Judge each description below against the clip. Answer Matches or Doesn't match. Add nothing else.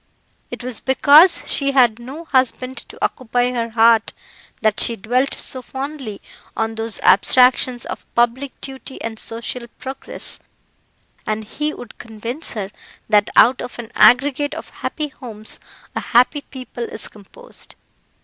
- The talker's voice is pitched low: Doesn't match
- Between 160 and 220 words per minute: Doesn't match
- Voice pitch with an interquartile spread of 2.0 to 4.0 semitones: Matches